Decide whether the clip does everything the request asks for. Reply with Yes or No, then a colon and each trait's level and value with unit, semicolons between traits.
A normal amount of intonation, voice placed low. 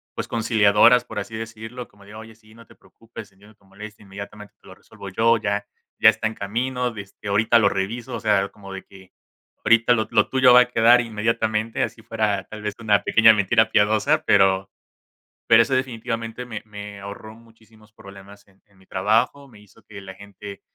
No: narrow, 2.2 semitones; low, 110 Hz